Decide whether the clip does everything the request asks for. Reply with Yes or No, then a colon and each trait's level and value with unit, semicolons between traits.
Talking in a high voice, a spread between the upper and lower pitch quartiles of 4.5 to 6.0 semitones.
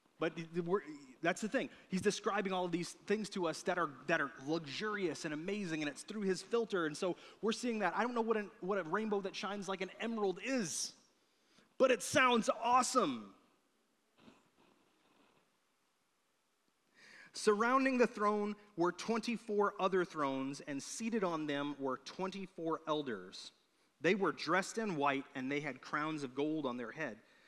Yes: high, 195 Hz; wide, 5.5 semitones